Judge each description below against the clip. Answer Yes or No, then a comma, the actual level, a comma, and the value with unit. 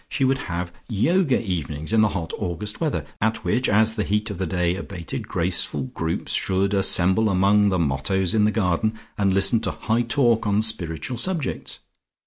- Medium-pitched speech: No, low, 100 Hz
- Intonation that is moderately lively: Yes, average, 3.9 semitones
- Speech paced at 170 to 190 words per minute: Yes, average, 180 wpm